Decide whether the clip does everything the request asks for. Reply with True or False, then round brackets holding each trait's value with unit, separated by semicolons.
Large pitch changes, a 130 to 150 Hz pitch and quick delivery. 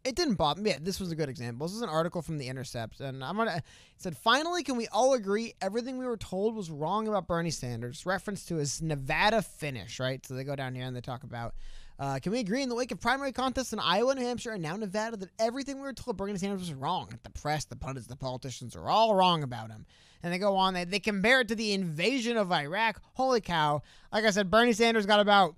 False (8.4 semitones; 190 Hz; 260 wpm)